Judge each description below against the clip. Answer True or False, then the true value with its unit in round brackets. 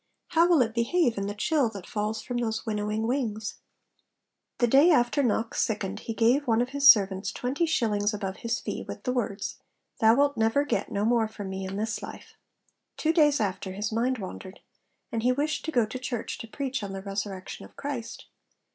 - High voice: True (225 Hz)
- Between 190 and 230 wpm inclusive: True (200 wpm)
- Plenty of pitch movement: False (4.0 semitones)